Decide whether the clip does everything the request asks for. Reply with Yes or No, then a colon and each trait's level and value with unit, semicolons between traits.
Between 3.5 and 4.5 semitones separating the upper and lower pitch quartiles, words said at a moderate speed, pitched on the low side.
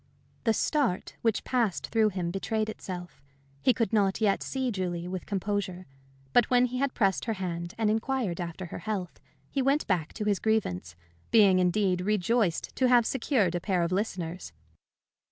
No: average, 4.0 semitones; average, 170 wpm; high, 200 Hz